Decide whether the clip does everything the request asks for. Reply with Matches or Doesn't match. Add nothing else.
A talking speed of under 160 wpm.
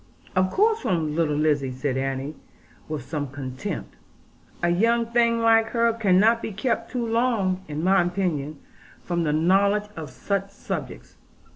Matches